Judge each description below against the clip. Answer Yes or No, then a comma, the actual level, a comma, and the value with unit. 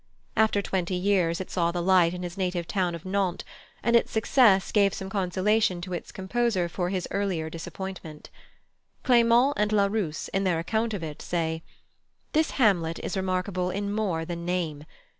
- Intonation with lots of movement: No, average, 2.9 semitones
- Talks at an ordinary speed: Yes, average, 170 wpm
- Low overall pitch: No, medium, 185 Hz